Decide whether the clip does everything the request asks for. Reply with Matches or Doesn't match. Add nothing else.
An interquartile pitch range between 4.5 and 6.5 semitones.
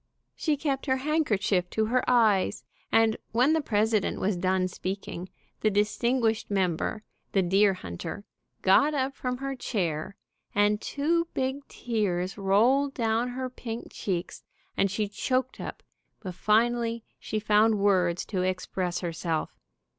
Matches